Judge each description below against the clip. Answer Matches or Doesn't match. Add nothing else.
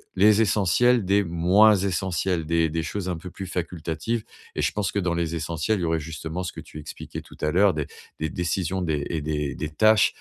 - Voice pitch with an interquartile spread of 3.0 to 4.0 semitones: Matches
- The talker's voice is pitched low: Matches